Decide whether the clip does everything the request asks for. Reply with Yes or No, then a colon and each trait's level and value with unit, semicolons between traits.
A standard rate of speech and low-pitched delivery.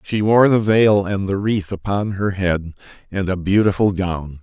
Yes: average, 190 wpm; low, 100 Hz